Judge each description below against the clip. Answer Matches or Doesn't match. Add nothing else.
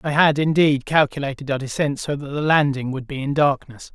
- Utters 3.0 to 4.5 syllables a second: Doesn't match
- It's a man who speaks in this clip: Matches